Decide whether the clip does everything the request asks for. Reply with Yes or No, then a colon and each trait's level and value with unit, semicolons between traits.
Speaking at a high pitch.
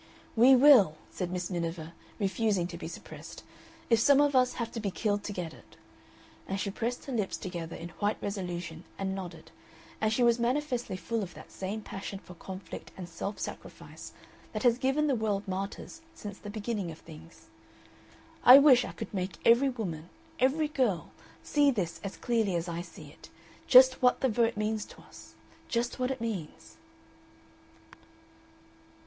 Yes: high, 210 Hz